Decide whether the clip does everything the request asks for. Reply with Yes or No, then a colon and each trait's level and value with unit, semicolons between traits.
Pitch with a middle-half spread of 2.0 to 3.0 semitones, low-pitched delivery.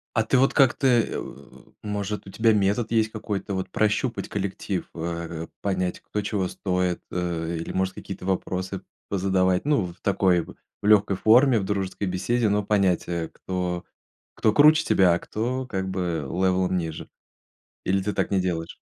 Yes: average, 2.7 semitones; very low, 95 Hz